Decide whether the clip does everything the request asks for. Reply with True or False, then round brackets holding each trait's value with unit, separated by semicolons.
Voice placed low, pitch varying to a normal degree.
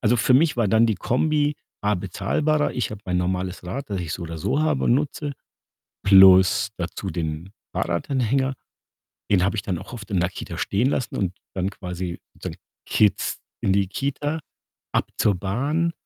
False (100 Hz; 6.6 semitones)